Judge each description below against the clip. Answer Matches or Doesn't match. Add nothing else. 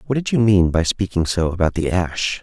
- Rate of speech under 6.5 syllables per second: Matches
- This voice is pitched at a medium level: Doesn't match